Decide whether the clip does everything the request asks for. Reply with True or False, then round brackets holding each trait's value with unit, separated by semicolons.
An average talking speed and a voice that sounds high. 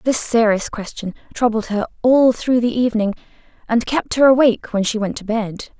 True (185 wpm; 230 Hz)